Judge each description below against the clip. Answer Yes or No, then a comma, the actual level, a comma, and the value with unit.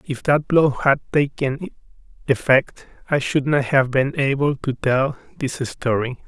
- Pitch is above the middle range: No, low, 135 Hz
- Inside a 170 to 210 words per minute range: No, average, 155 wpm